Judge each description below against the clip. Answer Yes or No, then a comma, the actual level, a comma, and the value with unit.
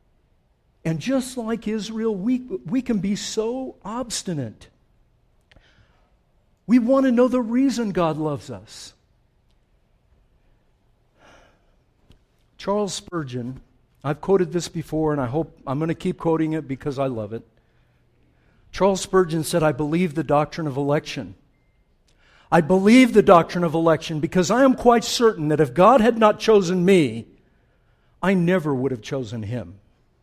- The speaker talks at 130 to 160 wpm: Yes, average, 140 wpm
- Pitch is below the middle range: No, medium, 165 Hz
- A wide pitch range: Yes, wide, 7.2 semitones